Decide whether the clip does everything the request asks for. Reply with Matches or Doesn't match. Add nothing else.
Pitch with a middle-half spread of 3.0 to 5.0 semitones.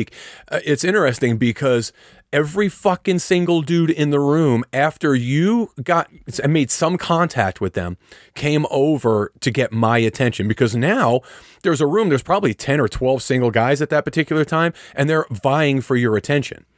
Matches